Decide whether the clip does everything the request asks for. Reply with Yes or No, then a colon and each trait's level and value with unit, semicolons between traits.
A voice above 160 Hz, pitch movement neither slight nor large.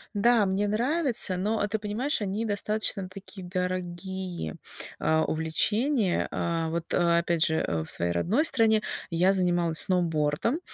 Yes: high, 190 Hz; average, 4.2 semitones